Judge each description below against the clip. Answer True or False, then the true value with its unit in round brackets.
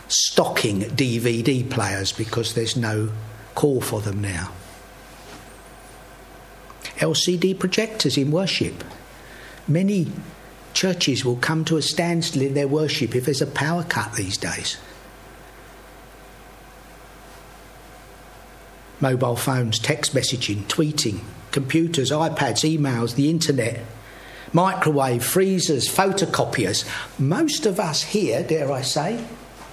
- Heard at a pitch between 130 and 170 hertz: True (140 Hz)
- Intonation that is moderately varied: False (6.2 semitones)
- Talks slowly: True (105 wpm)